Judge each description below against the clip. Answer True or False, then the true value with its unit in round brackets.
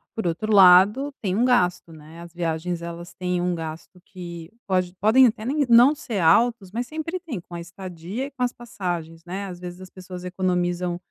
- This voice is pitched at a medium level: True (180 Hz)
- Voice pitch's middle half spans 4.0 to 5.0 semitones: True (4.7 semitones)